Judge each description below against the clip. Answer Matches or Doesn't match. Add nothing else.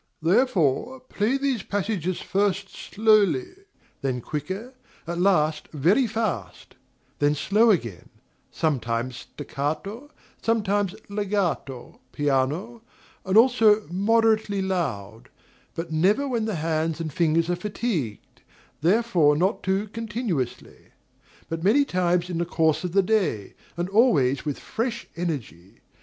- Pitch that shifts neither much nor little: Doesn't match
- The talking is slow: Matches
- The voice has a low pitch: Doesn't match